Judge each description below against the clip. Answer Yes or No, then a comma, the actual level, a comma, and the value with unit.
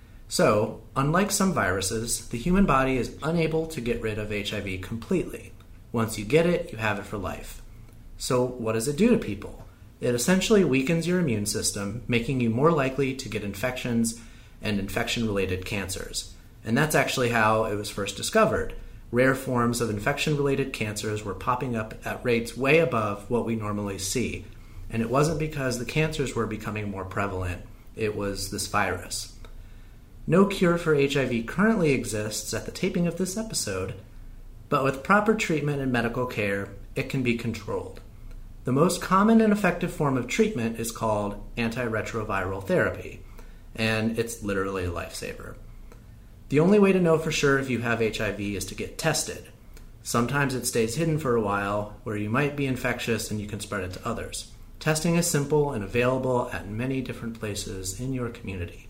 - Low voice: Yes, low, 115 Hz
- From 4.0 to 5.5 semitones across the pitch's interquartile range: Yes, average, 4.6 semitones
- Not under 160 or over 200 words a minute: Yes, average, 175 wpm